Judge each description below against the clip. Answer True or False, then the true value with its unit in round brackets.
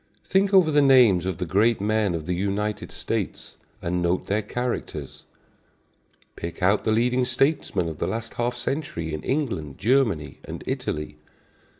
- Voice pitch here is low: True (105 Hz)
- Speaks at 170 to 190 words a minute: False (160 wpm)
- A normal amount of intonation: False (6.0 semitones)